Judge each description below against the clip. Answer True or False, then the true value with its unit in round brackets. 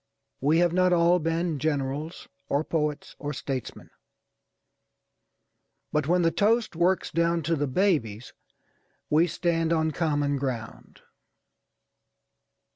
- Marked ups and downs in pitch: False (3.1 semitones)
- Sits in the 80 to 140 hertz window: False (160 Hz)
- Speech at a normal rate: False (115 wpm)